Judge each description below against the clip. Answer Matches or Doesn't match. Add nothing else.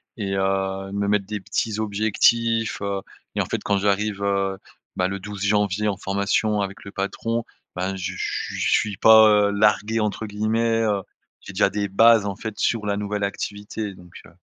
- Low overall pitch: Matches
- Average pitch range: Doesn't match